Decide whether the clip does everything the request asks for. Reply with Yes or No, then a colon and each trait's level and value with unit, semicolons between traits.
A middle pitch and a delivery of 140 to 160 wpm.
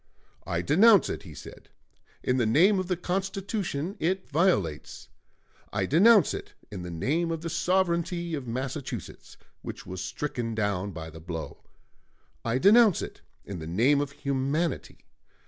Yes: medium, 150 Hz; average, 150 wpm